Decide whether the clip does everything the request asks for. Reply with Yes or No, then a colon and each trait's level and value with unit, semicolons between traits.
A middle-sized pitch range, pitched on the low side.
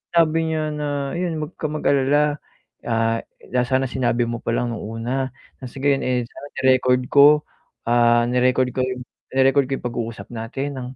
Yes: average, 3.1 semitones; low, 130 Hz